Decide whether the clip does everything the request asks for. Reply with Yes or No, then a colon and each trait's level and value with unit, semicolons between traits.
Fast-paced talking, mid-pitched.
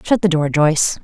Yes: fast, 235 wpm; medium, 165 Hz